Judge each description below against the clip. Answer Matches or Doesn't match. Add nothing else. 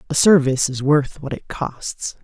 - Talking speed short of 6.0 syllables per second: Matches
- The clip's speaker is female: Doesn't match